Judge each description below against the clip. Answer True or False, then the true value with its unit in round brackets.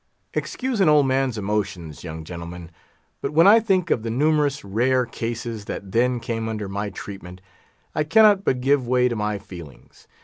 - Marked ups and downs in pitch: True (6.3 semitones)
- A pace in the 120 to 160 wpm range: False (175 wpm)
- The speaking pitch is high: False (115 Hz)